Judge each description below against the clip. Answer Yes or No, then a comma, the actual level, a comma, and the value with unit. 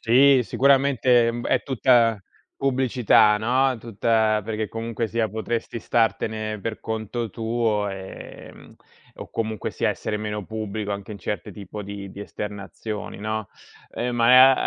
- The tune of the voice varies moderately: No, narrow, 2.2 semitones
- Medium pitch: No, low, 110 Hz